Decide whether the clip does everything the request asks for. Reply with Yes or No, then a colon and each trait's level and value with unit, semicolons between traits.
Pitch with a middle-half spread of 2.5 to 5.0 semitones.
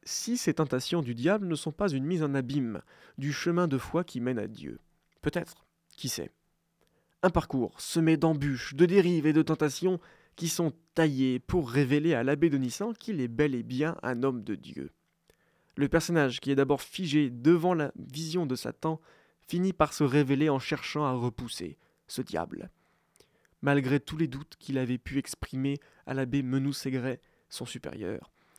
Yes: average, 3.9 semitones